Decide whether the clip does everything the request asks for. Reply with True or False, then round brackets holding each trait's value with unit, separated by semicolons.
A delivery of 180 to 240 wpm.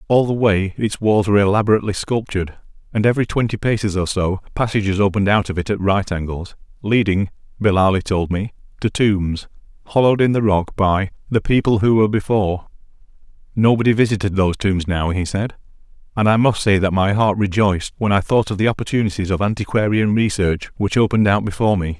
True (185 wpm)